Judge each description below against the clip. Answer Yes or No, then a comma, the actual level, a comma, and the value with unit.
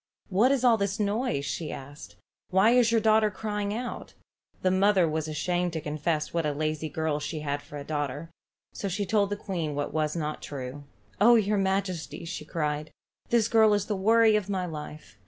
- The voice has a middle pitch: Yes, medium, 180 Hz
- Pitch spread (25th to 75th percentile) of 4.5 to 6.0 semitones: Yes, wide, 5.5 semitones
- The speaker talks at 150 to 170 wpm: No, average, 195 wpm